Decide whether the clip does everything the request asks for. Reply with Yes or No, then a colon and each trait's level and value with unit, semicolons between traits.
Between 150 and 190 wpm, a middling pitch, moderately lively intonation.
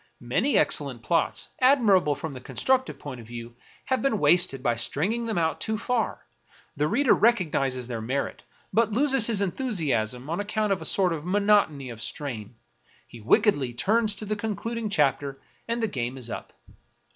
No: average, 170 wpm; medium, 175 Hz; wide, 9.0 semitones